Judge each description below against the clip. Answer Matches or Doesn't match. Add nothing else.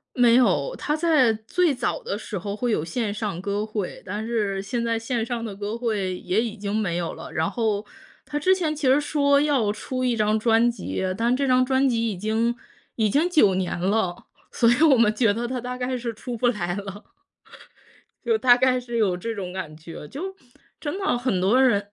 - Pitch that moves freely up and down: Doesn't match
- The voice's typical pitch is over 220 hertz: Matches